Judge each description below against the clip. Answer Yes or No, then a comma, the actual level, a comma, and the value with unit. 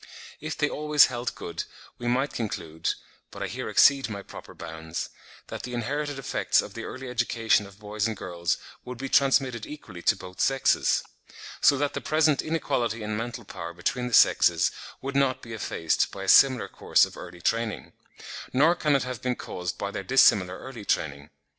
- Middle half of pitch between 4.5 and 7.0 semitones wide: Yes, wide, 5.4 semitones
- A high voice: No, low, 120 Hz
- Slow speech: No, average, 185 wpm